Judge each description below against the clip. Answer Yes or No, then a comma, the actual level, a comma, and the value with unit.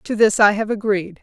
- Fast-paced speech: Yes, fast, 245 wpm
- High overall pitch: Yes, high, 205 Hz